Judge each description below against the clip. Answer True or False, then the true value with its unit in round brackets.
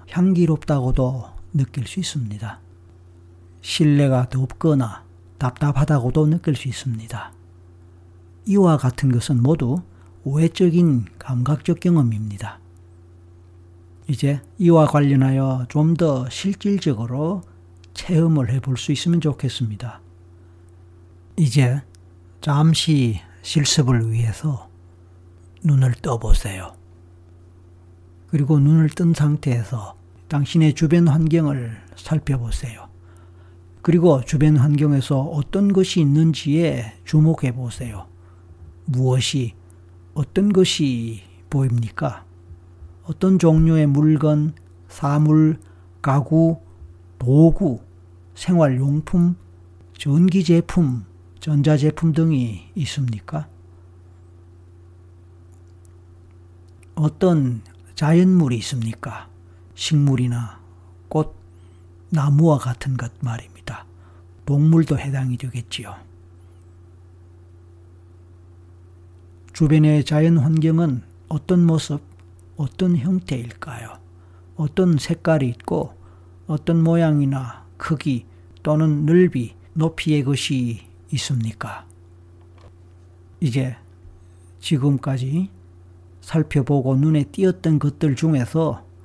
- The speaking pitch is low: True (125 Hz)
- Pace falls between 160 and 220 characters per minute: True (195 characters per minute)